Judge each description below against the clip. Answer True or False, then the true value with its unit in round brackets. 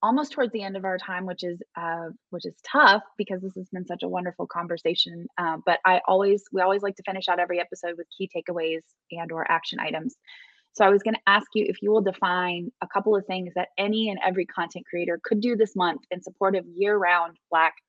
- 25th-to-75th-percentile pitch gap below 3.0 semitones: True (2.6 semitones)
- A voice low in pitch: False (185 Hz)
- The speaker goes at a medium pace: False (235 wpm)